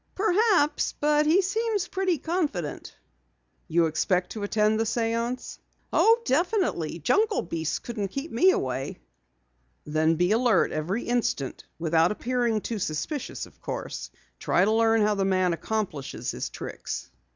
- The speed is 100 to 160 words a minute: Yes, average, 140 wpm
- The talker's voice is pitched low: No, high, 225 Hz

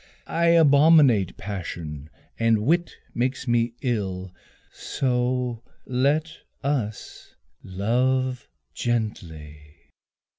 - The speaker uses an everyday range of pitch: Yes, average, 4.9 semitones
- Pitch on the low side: Yes, low, 120 Hz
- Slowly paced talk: Yes, slow, 75 wpm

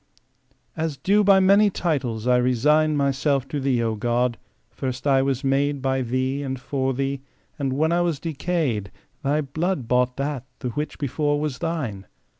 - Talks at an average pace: Yes, average, 170 wpm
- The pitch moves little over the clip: No, average, 3.3 semitones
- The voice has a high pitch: No, low, 135 Hz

